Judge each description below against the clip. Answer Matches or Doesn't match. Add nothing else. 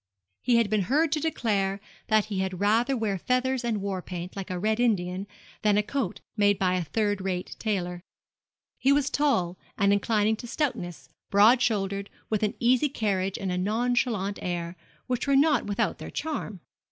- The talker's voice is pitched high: Matches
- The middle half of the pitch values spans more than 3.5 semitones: Matches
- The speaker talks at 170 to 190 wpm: Matches